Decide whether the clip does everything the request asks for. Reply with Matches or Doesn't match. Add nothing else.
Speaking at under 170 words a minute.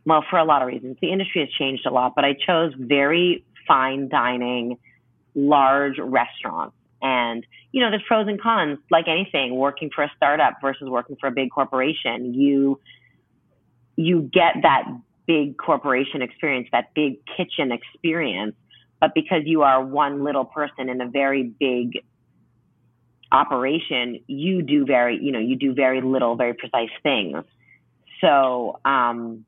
Matches